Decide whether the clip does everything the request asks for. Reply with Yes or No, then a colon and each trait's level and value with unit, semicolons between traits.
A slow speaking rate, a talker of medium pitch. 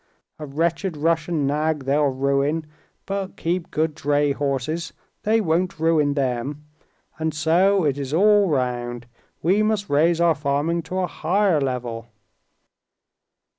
Yes: slow, 130 wpm; medium, 155 Hz